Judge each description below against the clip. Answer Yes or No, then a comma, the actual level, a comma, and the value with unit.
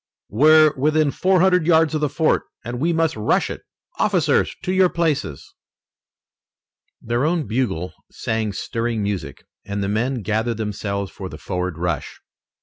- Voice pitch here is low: Yes, low, 120 Hz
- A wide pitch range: Yes, wide, 7.4 semitones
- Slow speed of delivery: No, average, 150 wpm